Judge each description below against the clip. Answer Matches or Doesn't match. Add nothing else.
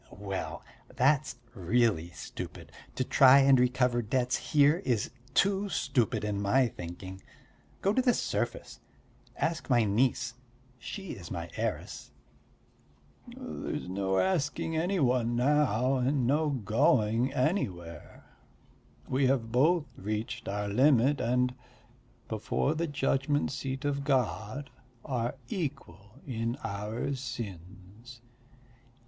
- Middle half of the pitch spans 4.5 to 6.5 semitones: Matches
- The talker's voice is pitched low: Matches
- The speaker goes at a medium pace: Doesn't match